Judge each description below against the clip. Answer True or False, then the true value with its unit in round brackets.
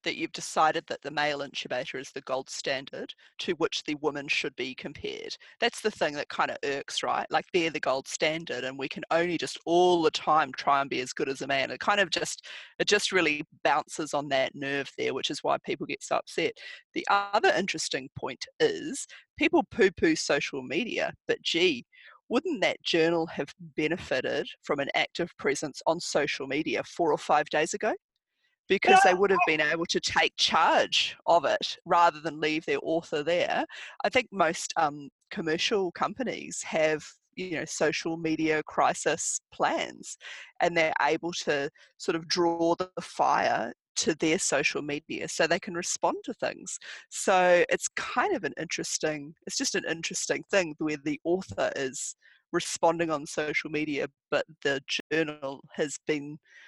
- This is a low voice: False (170 Hz)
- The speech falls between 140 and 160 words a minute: False (180 wpm)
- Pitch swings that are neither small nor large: False (6.4 semitones)